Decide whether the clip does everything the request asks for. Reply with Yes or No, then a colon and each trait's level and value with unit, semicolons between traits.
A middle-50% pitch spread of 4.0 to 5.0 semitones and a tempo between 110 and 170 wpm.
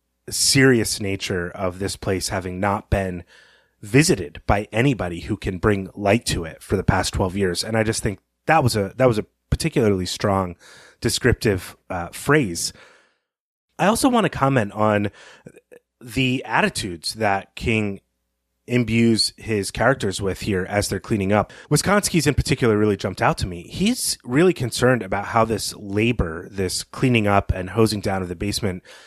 Yes: average, 4.5 semitones; average, 165 wpm